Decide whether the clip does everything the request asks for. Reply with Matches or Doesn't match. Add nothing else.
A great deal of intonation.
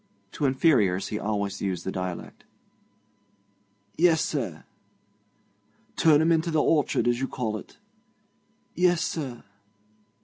Matches